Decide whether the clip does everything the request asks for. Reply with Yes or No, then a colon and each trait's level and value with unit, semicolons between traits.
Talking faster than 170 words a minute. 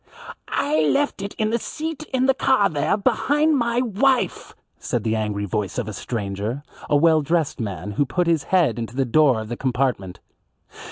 Yes: average, 185 wpm